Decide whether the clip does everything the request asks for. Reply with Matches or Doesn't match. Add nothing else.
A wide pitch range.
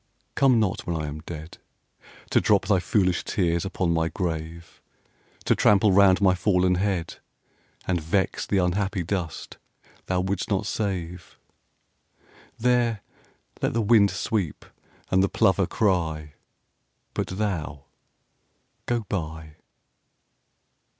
Doesn't match